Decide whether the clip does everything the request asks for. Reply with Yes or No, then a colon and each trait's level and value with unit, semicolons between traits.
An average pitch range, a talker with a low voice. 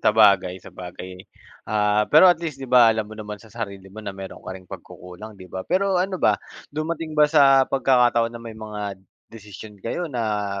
Yes: average, 4.9 semitones; low, 110 Hz